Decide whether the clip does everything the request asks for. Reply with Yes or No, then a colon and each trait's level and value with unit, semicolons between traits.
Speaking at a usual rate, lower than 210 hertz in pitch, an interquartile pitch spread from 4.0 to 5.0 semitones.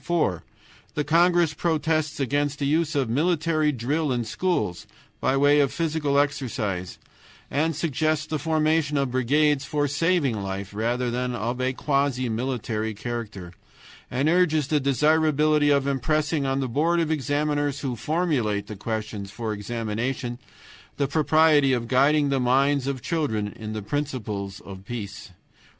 Yes: average, 145 wpm; medium, 140 Hz; average, 4.5 semitones